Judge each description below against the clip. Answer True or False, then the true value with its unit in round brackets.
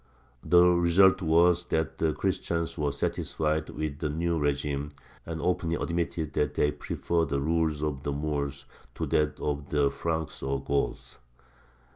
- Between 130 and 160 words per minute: True (150 wpm)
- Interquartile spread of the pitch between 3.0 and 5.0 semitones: False (2.5 semitones)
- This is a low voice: True (80 Hz)